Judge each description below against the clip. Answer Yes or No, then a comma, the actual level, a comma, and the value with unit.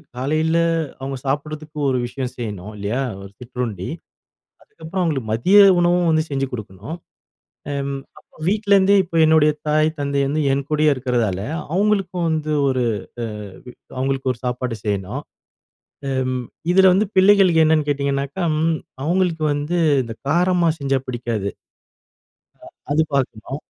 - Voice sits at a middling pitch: Yes, medium, 145 Hz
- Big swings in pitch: No, average, 4.6 semitones